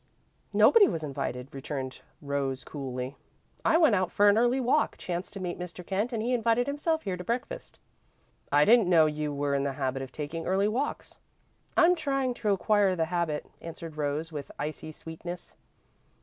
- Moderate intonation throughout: No, wide, 7.8 semitones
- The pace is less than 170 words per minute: No, average, 175 wpm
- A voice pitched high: No, medium, 175 Hz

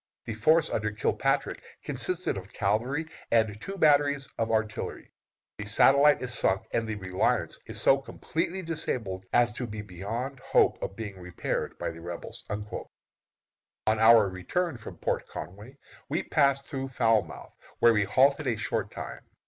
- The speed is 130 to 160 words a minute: Yes, average, 150 wpm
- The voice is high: No, low, 115 Hz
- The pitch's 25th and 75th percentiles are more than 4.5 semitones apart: Yes, average, 5.0 semitones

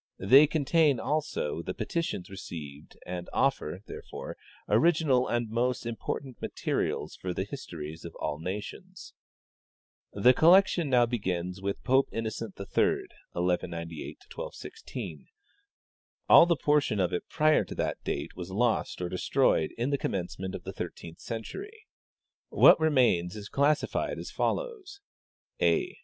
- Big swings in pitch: Yes, wide, 8.4 semitones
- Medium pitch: No, low, 115 Hz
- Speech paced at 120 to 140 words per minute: Yes, slow, 135 wpm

